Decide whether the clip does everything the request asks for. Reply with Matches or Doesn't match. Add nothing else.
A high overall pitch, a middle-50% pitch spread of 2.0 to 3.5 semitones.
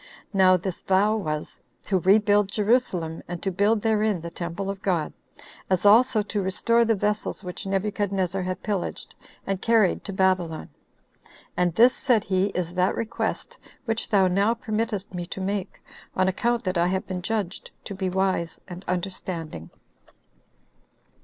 Matches